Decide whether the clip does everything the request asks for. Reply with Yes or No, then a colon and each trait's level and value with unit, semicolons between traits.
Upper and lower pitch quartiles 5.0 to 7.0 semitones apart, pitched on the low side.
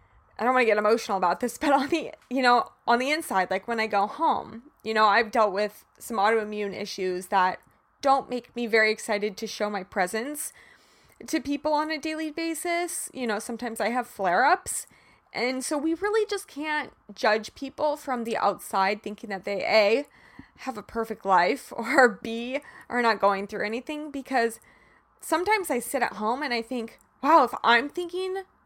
No: wide, 5.4 semitones; high, 235 Hz